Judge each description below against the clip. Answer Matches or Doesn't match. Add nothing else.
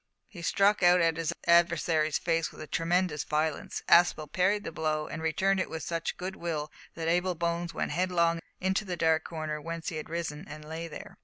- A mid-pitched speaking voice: Matches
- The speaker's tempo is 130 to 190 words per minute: Doesn't match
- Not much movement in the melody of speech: Matches